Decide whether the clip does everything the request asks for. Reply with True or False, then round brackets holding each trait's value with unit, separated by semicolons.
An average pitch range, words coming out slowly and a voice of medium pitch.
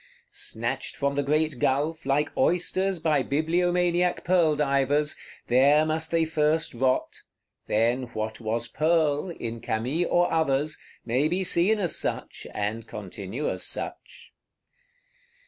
True (4.3 semitones; 130 wpm; 150 Hz)